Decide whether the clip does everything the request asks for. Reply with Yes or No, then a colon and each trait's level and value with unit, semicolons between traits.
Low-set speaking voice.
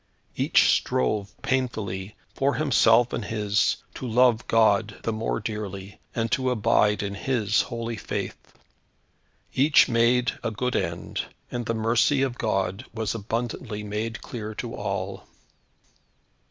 Yes: low, 115 Hz